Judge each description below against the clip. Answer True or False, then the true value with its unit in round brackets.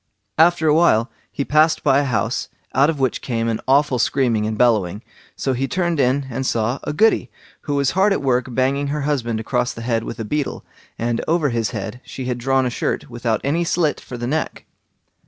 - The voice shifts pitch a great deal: False (3.8 semitones)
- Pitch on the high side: False (130 Hz)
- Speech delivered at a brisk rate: True (210 wpm)